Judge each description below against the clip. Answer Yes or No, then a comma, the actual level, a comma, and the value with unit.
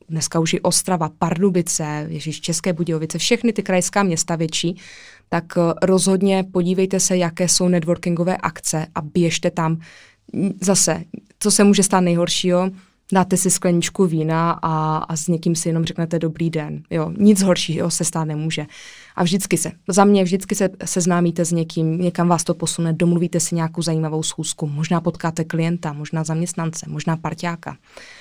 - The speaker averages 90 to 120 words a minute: No, average, 160 wpm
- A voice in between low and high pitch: Yes, medium, 170 Hz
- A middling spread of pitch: No, narrow, 2.1 semitones